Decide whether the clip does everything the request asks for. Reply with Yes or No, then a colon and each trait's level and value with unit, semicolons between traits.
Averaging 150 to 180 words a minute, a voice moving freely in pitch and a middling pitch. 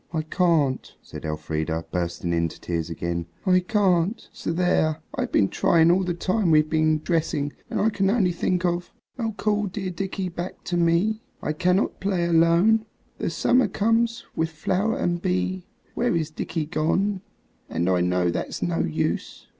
Yes: average, 170 wpm; wide, 6.5 semitones; medium, 170 Hz